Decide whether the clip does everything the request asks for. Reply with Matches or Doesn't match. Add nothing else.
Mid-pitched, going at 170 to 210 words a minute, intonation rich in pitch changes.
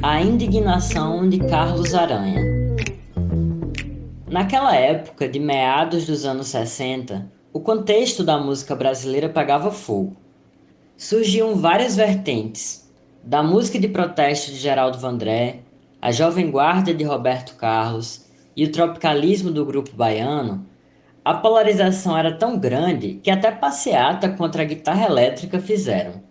Doesn't match